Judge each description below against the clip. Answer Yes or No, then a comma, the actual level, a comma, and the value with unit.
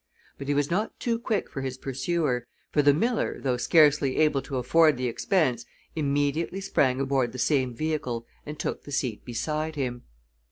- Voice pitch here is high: No, medium, 140 Hz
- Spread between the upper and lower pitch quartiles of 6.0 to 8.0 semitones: No, average, 3.5 semitones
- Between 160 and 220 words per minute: Yes, average, 175 wpm